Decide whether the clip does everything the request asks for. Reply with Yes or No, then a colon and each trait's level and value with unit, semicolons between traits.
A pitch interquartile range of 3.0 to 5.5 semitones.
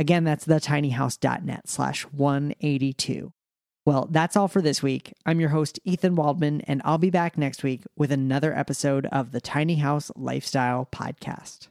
No: narrow, 2.6 semitones